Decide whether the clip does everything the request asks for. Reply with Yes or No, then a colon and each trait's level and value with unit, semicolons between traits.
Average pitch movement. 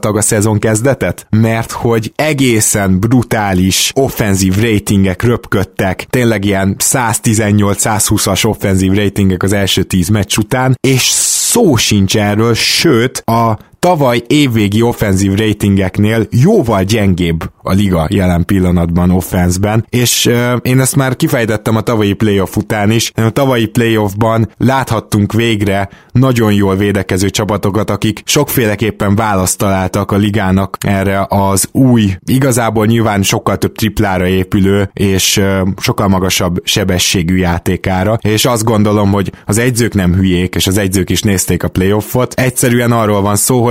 Yes: average, 3.0 semitones